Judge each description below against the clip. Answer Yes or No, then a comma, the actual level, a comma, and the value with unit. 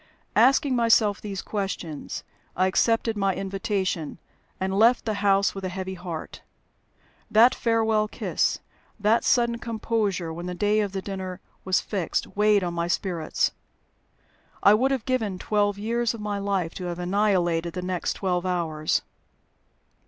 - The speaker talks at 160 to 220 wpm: No, average, 150 wpm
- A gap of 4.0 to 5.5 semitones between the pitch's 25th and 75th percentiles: No, average, 3.0 semitones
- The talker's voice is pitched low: No, high, 200 Hz